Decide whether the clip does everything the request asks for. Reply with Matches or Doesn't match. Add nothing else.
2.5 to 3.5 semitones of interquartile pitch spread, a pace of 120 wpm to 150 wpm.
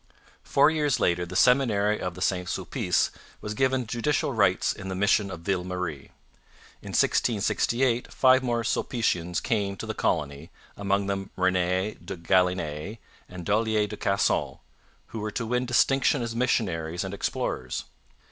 Doesn't match